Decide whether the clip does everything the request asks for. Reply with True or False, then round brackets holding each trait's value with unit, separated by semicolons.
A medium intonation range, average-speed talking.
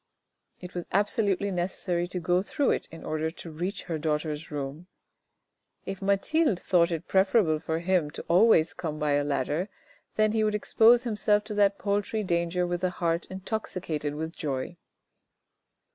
True (4.0 semitones; 160 wpm)